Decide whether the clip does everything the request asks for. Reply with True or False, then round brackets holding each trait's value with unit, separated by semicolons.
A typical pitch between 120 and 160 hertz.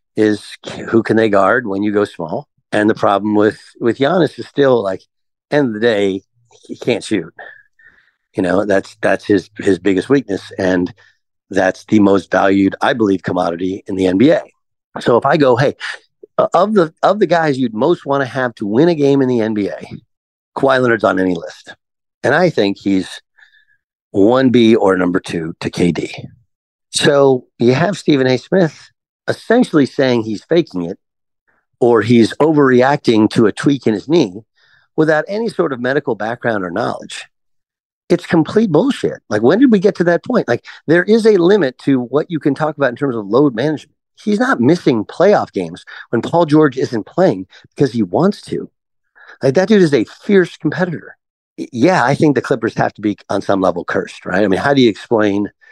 True (135 Hz)